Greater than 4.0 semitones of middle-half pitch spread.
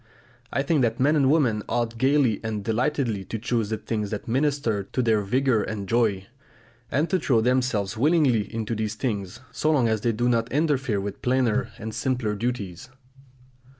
No: average, 3.6 semitones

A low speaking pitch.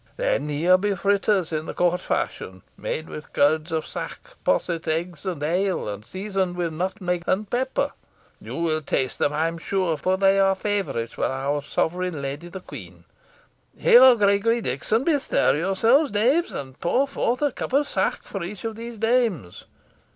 No: medium, 185 Hz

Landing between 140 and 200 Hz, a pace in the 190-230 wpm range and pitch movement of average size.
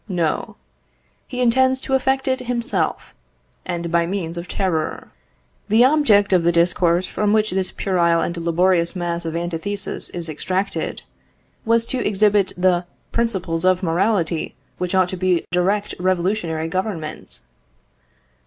No: medium, 185 Hz; slow, 135 wpm; average, 3.6 semitones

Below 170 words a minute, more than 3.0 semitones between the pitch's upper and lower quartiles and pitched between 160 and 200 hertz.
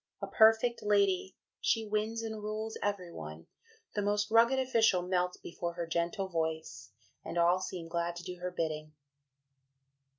Yes: average, 155 wpm; average, 4.2 semitones; medium, 185 Hz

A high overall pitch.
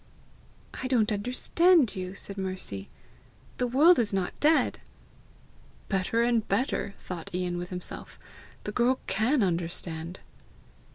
Yes: high, 200 Hz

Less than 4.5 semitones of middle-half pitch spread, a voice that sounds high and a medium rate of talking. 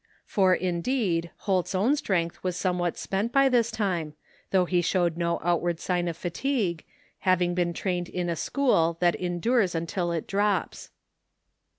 No: narrow, 2.5 semitones; medium, 180 Hz; average, 155 wpm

